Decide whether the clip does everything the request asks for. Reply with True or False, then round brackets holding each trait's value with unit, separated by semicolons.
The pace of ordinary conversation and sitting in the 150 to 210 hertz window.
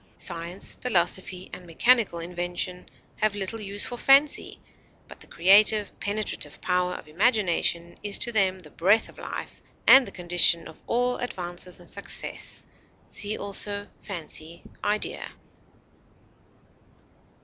False (125 wpm; 190 Hz)